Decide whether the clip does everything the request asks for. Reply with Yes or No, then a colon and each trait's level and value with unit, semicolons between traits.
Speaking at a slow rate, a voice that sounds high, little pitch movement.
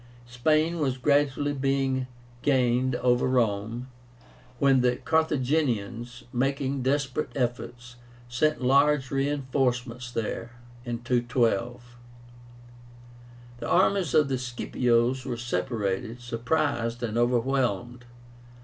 No: slow, 95 wpm; low, 125 Hz; narrow, 2.3 semitones